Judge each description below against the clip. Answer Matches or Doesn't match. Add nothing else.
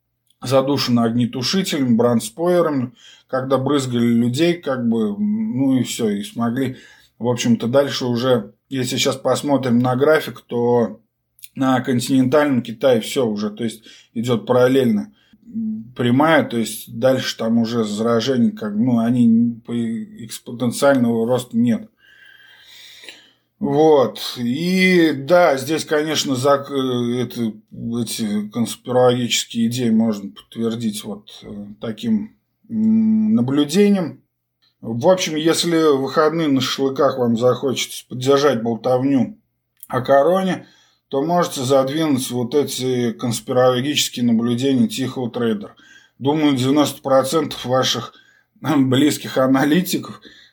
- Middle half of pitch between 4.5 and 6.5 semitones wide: Matches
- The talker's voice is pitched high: Doesn't match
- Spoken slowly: Matches